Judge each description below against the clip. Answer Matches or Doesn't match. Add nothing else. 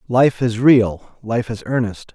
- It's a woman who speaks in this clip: Doesn't match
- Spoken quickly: Doesn't match